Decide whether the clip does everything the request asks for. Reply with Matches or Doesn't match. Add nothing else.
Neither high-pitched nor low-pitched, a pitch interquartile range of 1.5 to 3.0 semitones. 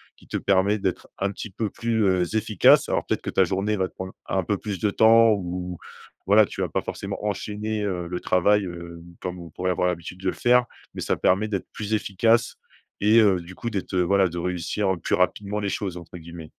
Doesn't match